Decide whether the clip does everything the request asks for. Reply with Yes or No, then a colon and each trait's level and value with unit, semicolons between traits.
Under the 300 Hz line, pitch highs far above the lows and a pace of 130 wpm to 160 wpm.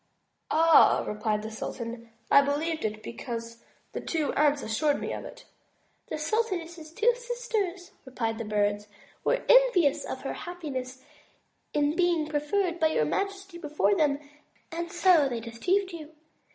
No: very high, 310 Hz; wide, 6.9 semitones; average, 145 wpm